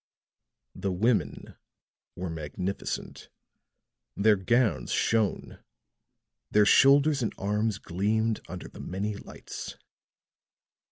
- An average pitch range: Yes, average, 3.4 semitones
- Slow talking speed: Yes, slow, 90 wpm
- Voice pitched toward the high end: No, low, 105 Hz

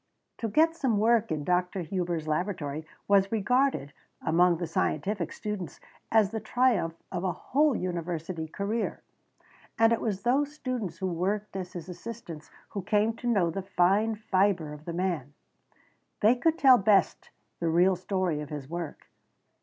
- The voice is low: No, high, 190 Hz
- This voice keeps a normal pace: Yes, average, 160 wpm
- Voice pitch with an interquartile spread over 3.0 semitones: Yes, average, 4.6 semitones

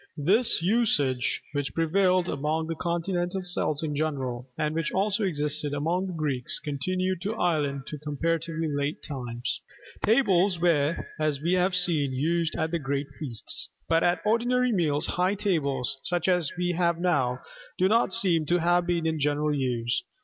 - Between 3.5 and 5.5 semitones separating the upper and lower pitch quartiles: Yes, average, 3.8 semitones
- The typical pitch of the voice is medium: Yes, medium, 165 Hz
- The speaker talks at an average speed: Yes, average, 165 wpm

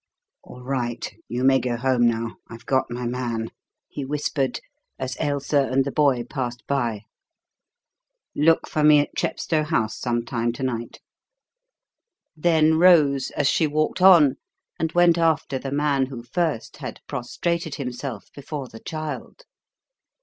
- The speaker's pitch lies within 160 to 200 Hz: No, low, 135 Hz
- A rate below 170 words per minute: Yes, average, 145 wpm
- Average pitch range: Yes, average, 4.0 semitones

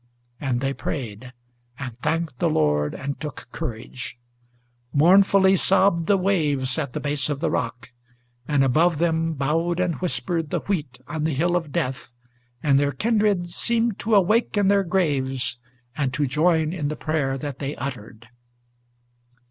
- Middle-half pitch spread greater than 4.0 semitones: Yes, average, 4.7 semitones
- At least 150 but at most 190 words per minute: Yes, average, 155 wpm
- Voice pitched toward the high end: No, medium, 150 Hz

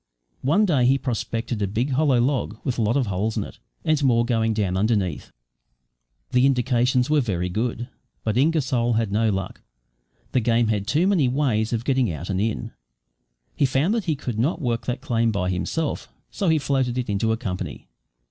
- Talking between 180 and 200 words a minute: Yes, average, 195 wpm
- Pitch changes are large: No, average, 3.7 semitones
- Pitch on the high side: No, low, 120 Hz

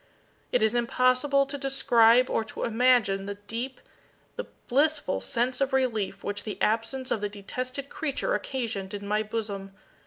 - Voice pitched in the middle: No, high, 235 Hz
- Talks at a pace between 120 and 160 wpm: Yes, average, 155 wpm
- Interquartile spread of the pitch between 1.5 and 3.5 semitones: No, average, 4.0 semitones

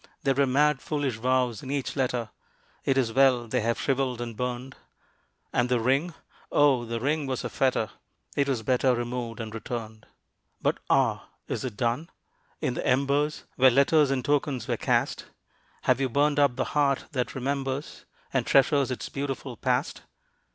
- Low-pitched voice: Yes, low, 130 Hz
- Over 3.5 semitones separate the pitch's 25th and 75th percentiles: No, narrow, 2.4 semitones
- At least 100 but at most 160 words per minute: No, average, 170 wpm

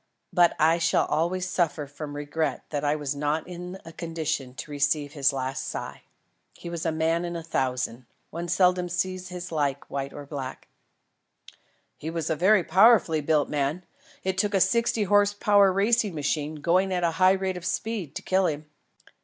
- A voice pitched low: No, medium, 165 Hz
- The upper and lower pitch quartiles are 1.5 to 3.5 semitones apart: No, average, 4.0 semitones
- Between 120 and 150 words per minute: No, average, 185 wpm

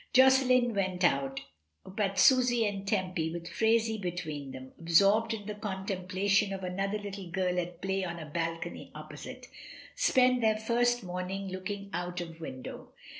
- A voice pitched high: Yes, high, 195 Hz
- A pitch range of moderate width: Yes, average, 3.6 semitones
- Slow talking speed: No, average, 160 wpm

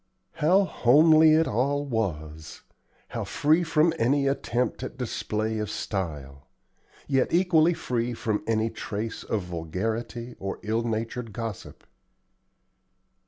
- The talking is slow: Yes, slow, 120 wpm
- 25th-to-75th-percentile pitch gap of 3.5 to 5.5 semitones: Yes, average, 5.1 semitones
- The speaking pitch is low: Yes, low, 115 Hz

